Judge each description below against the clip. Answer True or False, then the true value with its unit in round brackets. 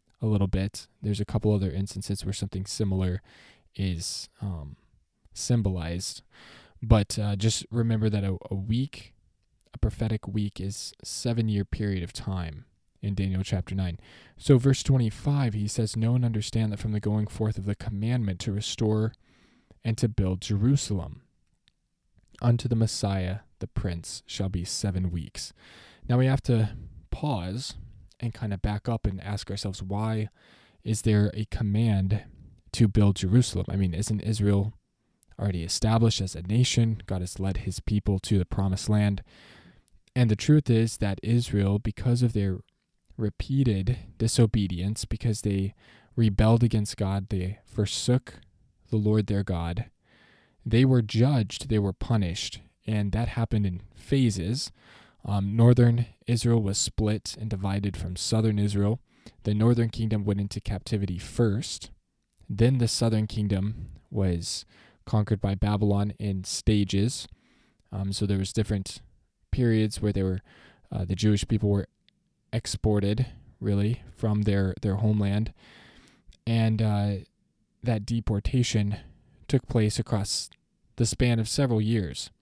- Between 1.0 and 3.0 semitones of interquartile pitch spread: True (2.7 semitones)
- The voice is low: True (105 Hz)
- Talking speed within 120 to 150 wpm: True (140 wpm)